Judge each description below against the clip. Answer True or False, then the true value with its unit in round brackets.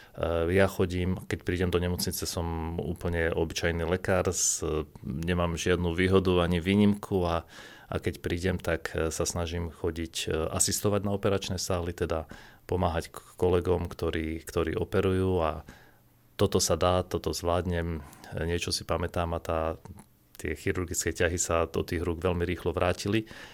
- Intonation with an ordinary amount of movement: False (1.9 semitones)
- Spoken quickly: False (140 wpm)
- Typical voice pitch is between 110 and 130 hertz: False (90 Hz)